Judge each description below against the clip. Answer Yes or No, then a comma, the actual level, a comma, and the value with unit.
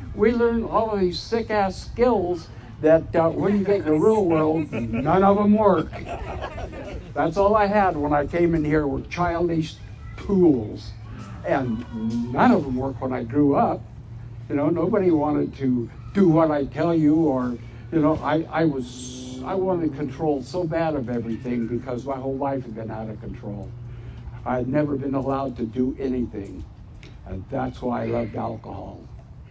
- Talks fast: No, average, 180 wpm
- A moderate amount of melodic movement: No, wide, 5.8 semitones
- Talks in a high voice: No, low, 135 Hz